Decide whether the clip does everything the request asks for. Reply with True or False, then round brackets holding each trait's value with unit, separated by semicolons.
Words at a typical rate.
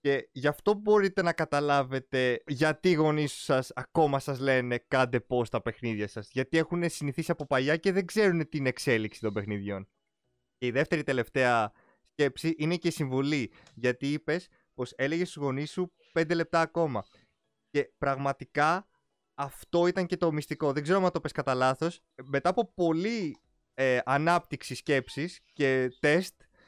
True (155 wpm)